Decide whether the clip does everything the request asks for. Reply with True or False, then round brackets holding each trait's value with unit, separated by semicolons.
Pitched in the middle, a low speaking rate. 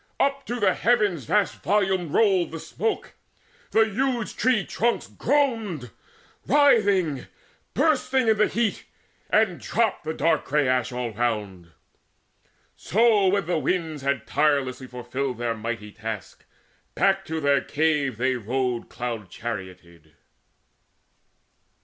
True (155 Hz; 125 wpm)